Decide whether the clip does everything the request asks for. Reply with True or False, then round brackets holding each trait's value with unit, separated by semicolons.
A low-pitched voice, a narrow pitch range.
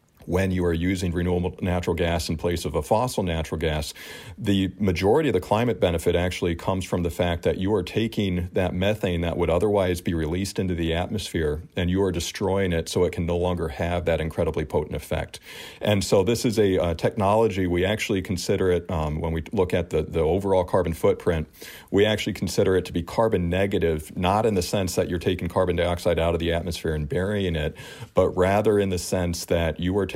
True (90 Hz; 2.3 semitones)